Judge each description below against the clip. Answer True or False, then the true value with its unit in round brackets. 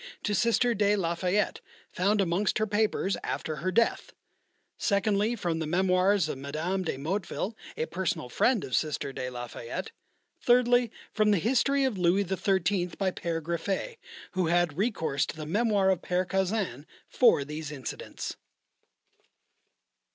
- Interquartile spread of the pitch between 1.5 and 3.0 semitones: False (4.3 semitones)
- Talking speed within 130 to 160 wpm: True (150 wpm)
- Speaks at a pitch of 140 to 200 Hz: True (190 Hz)